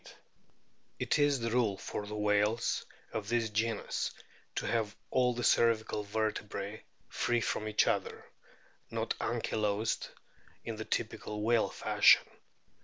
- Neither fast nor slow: No, slow, 125 wpm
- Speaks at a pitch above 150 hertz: No, low, 110 Hz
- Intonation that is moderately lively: No, narrow, 1.8 semitones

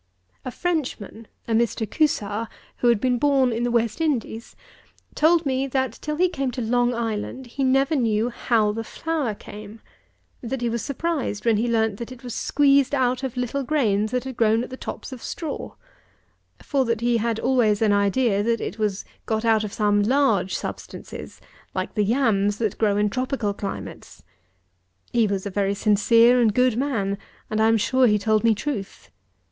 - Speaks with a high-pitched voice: Yes, high, 230 Hz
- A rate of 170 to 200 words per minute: Yes, average, 185 wpm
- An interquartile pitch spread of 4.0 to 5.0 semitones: No, average, 3.6 semitones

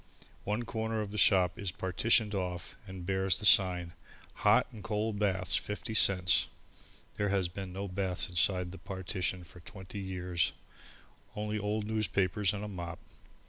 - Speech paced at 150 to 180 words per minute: Yes, average, 155 wpm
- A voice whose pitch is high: No, very low, 95 Hz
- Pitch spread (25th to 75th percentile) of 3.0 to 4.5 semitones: No, narrow, 2.4 semitones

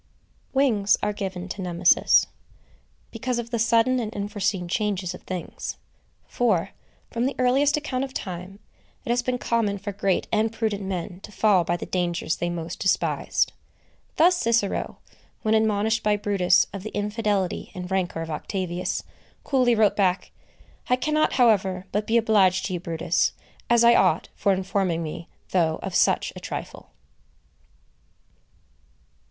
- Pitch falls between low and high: No, high, 205 Hz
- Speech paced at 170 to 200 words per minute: No, average, 150 wpm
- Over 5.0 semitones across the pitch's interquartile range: No, average, 4.0 semitones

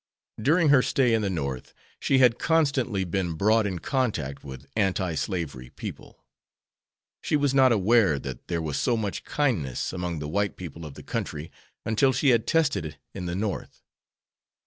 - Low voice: Yes, low, 100 Hz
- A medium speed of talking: Yes, average, 170 wpm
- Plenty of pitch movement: Yes, wide, 7.7 semitones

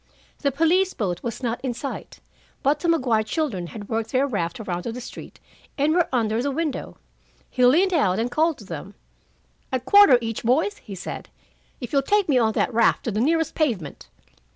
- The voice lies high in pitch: Yes, very high, 250 Hz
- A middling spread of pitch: No, wide, 5.9 semitones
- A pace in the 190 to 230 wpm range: Yes, average, 200 wpm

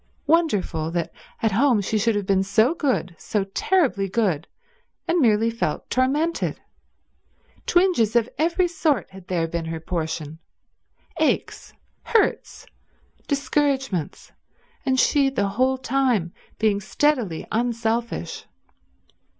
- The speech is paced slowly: Yes, slow, 115 wpm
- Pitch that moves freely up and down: Yes, wide, 6.3 semitones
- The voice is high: Yes, high, 230 Hz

